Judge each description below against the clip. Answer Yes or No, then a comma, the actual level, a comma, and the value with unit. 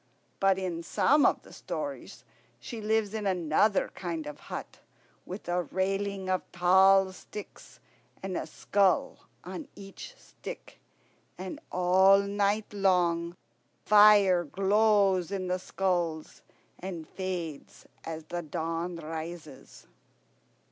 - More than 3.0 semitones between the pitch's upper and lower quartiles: No, narrow, 2.5 semitones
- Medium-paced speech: No, slow, 115 wpm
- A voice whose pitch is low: No, medium, 185 Hz